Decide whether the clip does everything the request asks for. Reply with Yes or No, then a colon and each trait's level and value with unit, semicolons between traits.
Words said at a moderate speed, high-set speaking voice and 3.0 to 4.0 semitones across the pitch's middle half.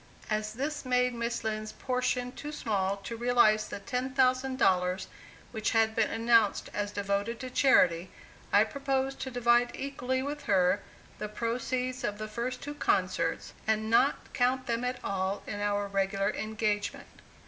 Yes: average, 150 wpm; high, 230 Hz; average, 3.6 semitones